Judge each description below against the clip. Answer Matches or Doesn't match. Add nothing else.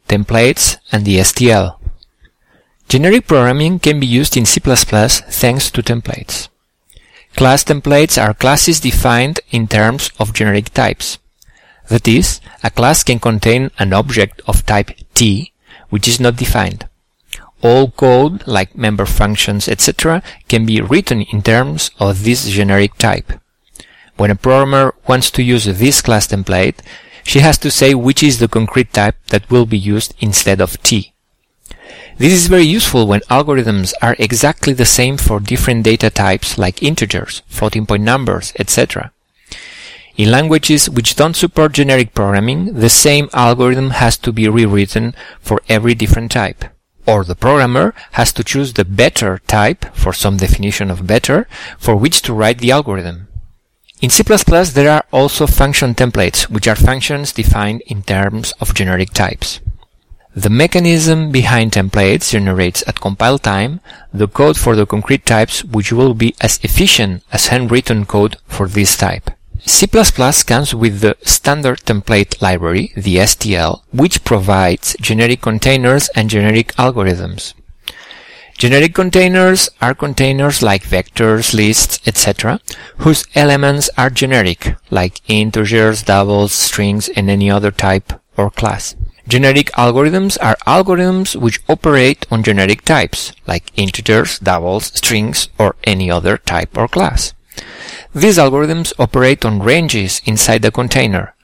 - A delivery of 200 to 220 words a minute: Doesn't match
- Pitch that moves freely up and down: Doesn't match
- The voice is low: Matches